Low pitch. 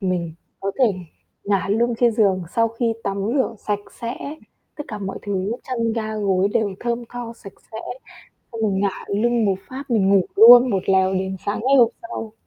No: high, 215 Hz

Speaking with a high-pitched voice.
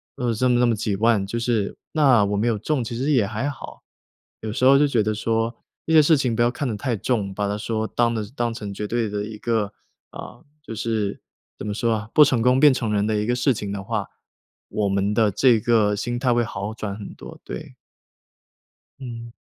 No: low, 115 Hz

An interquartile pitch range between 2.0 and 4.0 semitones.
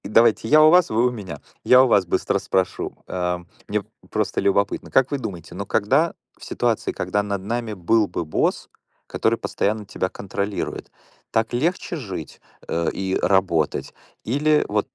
No: average, 4.7 semitones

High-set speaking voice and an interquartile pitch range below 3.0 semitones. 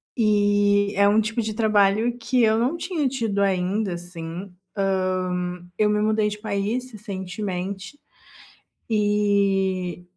Yes: high, 205 Hz; narrow, 2.4 semitones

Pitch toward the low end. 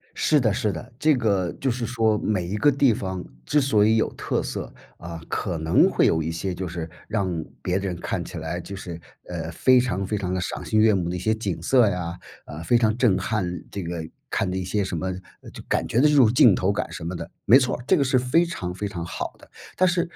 Yes: low, 100 Hz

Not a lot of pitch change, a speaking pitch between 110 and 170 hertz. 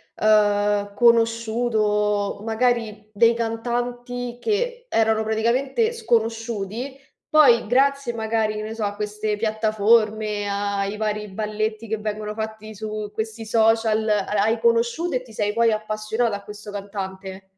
No: narrow, 1.9 semitones; high, 220 Hz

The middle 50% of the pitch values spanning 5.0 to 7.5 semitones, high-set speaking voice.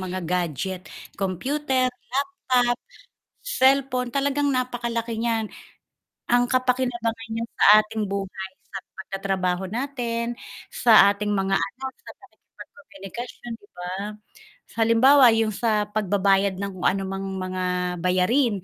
No: average, 4.5 semitones; high, 225 Hz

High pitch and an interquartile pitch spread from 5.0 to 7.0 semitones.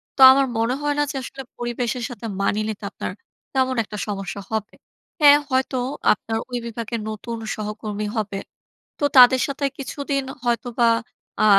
No: high, 235 Hz; average, 3.5 semitones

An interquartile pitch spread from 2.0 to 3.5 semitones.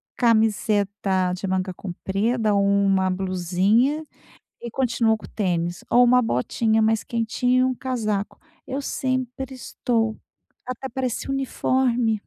No: average, 4.1 semitones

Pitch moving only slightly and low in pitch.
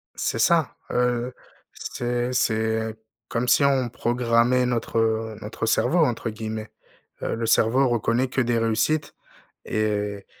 Yes: narrow, 1.9 semitones; low, 115 Hz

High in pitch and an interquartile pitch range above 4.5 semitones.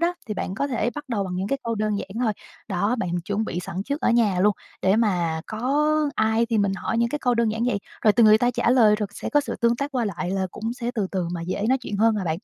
No: high, 220 Hz; average, 3.7 semitones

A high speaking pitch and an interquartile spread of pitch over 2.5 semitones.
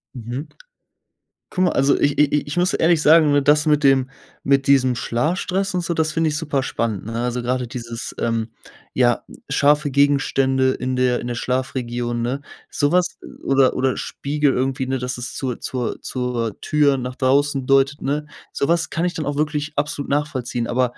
No: low, 135 Hz; average, 2.9 semitones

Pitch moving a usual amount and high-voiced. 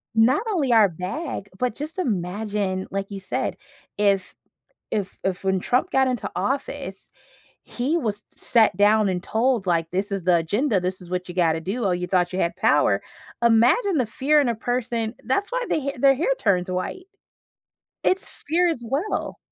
No: wide, 6.2 semitones; high, 220 Hz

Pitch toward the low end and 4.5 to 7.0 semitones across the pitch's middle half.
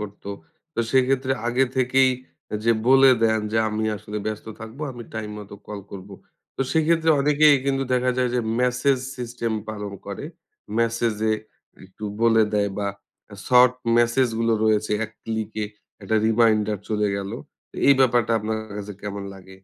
No: low, 115 Hz; average, 3.2 semitones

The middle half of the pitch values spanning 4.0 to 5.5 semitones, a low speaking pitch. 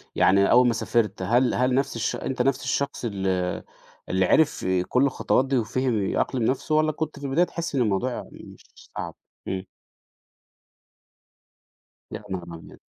Yes: average, 4.9 semitones; low, 125 Hz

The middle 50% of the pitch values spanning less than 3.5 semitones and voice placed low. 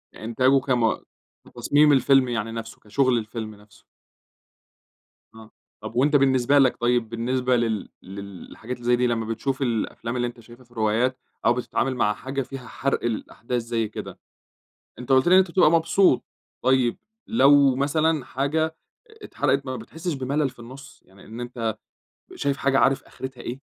Yes: average, 2.9 semitones; low, 125 Hz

